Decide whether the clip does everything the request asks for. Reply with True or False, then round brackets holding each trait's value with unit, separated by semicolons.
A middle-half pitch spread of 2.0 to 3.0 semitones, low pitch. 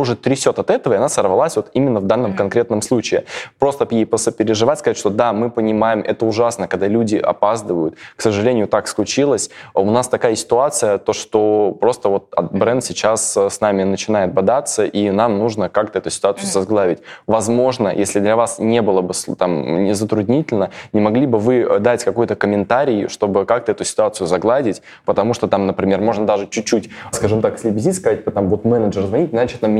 True (2.4 semitones; 110 Hz)